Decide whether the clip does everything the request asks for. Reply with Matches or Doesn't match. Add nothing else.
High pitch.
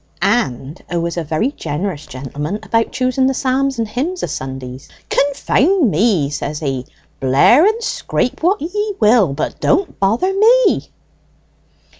Matches